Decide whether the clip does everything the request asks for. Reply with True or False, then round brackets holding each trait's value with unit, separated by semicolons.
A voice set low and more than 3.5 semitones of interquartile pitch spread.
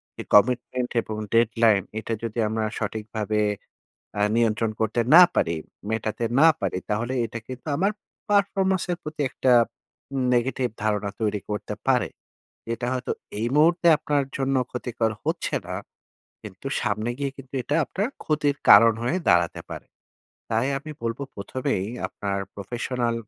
True (120 Hz; 4.2 semitones)